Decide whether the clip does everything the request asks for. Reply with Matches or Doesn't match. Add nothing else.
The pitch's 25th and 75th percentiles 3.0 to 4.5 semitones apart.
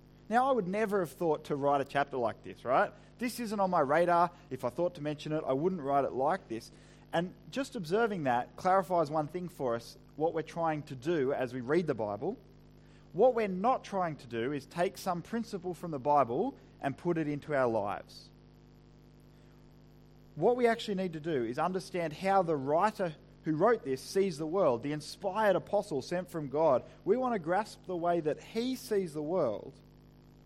Doesn't match